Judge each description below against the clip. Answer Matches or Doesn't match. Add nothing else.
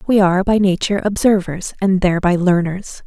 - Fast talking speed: Doesn't match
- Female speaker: Matches